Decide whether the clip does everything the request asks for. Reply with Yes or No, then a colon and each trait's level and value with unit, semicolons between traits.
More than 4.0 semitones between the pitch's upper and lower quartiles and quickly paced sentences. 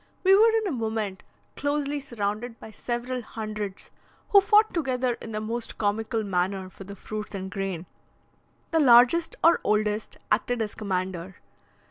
No: average, 4.4 semitones; average, 150 wpm